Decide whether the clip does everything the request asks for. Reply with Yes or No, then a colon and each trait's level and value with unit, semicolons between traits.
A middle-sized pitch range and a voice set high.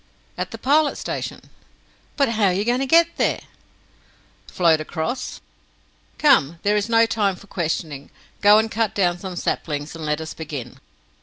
No: wide, 6.2 semitones; high, 195 Hz